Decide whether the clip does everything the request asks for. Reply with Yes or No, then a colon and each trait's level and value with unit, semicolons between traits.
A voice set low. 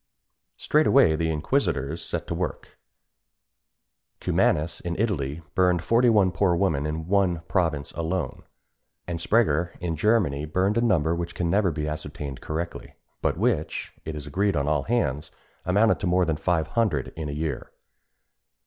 Yes: very low, 85 Hz